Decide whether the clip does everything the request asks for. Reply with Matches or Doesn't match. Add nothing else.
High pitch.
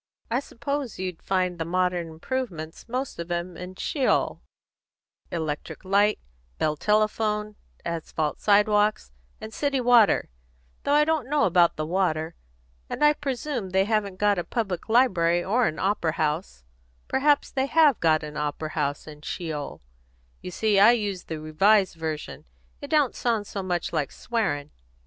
Matches